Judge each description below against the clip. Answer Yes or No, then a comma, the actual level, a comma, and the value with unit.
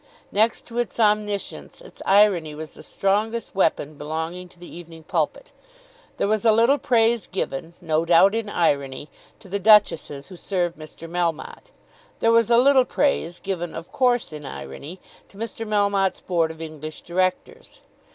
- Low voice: No, medium, 185 Hz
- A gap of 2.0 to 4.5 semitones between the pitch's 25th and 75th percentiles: No, average, 5.1 semitones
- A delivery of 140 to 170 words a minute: Yes, average, 160 wpm